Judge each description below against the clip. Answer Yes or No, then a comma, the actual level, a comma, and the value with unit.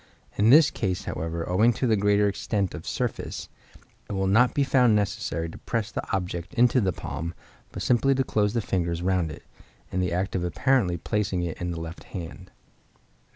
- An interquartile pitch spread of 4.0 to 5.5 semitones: Yes, average, 4.3 semitones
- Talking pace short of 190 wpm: No, average, 195 wpm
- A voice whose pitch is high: No, very low, 95 Hz